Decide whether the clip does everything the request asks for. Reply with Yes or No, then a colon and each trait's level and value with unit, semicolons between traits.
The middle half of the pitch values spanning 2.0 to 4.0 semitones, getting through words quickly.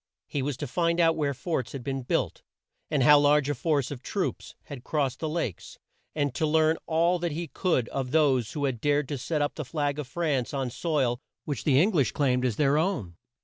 Yes: average, 3.3 semitones; fast, 225 wpm